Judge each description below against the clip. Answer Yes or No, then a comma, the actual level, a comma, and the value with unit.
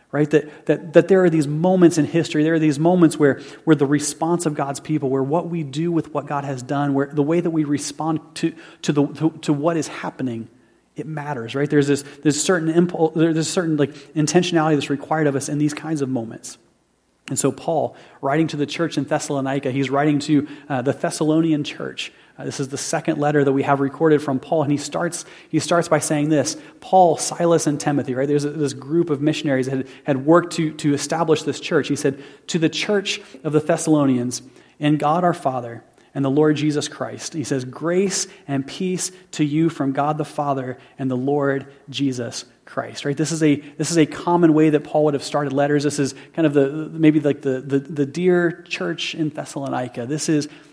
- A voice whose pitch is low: No, medium, 150 Hz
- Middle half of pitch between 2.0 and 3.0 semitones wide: Yes, narrow, 2.4 semitones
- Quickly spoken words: Yes, fast, 220 wpm